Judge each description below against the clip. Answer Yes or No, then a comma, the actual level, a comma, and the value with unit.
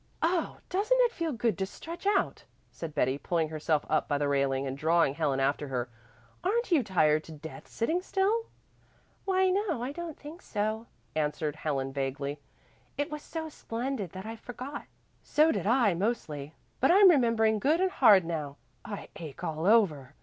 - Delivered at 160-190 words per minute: Yes, average, 175 wpm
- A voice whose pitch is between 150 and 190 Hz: No, high, 210 Hz